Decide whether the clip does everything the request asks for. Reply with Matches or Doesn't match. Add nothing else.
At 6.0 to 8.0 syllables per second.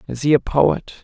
Doesn't match